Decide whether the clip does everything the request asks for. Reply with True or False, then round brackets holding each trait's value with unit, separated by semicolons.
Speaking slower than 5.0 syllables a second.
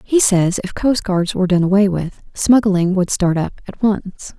True (4.5 syllables/s)